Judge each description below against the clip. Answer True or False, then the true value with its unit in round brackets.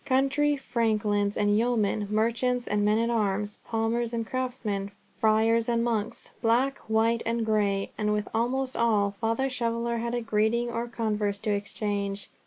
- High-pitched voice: True (225 Hz)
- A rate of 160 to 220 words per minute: False (150 wpm)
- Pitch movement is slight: True (2.2 semitones)